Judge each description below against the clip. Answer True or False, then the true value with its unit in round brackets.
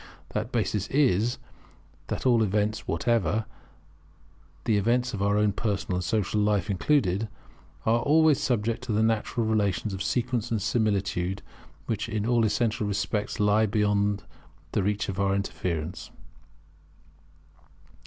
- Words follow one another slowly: True (130 wpm)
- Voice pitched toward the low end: True (105 Hz)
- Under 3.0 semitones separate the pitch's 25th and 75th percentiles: True (2.5 semitones)